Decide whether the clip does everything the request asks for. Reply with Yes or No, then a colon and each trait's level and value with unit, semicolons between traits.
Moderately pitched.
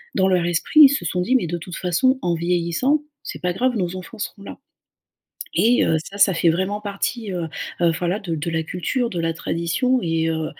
Yes: medium, 180 Hz